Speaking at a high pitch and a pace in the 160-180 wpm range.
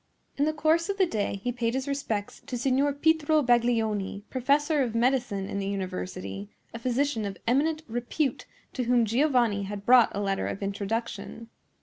Yes: high, 240 Hz; average, 175 wpm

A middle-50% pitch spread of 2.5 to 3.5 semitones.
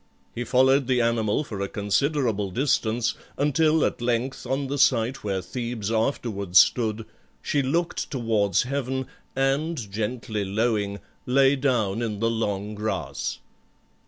No: average, 4.1 semitones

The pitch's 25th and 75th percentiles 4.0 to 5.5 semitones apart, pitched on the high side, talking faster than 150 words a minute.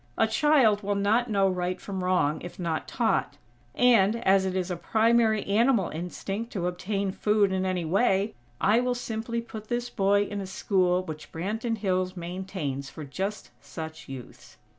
No: average, 3.3 semitones; high, 195 Hz; average, 170 wpm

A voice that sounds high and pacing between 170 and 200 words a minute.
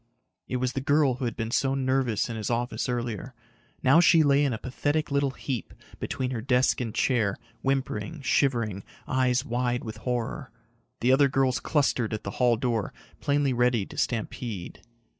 No: low, 125 Hz; average, 175 wpm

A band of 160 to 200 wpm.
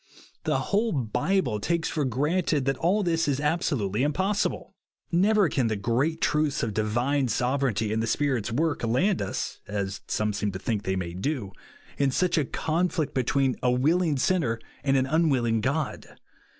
Yes: average, 170 wpm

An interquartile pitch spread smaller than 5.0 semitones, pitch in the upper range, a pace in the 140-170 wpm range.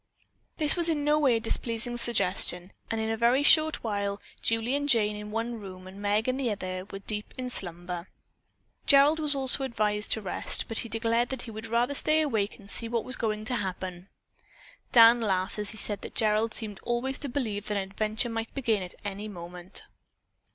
No: average, 3.3 semitones; high, 225 Hz; fast, 205 wpm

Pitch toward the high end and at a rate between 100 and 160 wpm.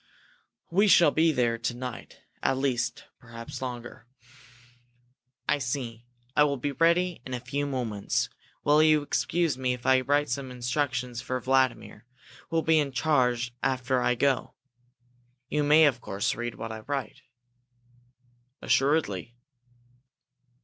No: low, 130 Hz; average, 140 wpm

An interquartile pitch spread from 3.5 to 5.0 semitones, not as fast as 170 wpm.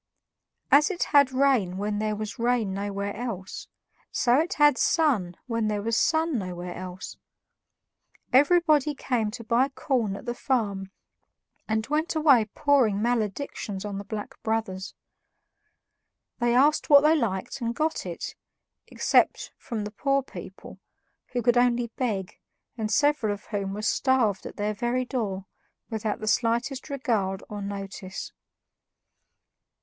Yes: average, 4.7 semitones; average, 140 wpm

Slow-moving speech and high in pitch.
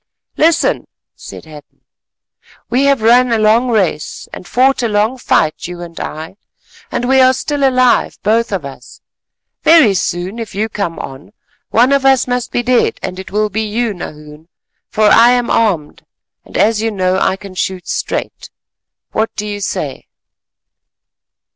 No: average, 165 wpm; high, 215 Hz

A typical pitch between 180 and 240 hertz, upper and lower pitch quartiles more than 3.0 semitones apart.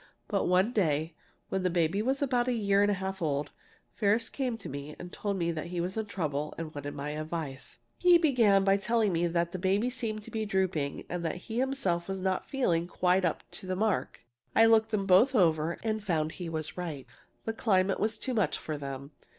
Yes: high, 190 Hz; average, 4.9 semitones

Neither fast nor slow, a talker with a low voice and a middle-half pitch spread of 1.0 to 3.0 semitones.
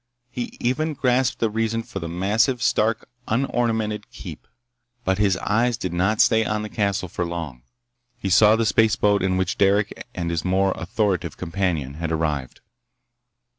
No: average, 160 wpm; low, 100 Hz; average, 3.9 semitones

